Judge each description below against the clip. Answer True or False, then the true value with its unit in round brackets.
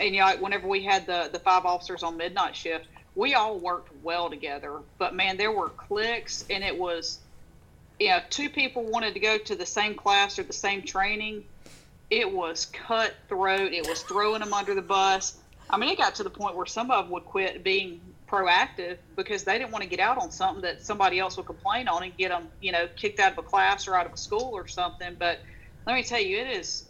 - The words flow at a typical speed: False (235 wpm)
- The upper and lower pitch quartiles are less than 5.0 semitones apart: True (3.2 semitones)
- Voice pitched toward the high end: True (195 Hz)